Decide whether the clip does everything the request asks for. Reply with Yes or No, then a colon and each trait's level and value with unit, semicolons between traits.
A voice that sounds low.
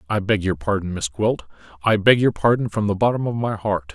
Yes: low, 105 Hz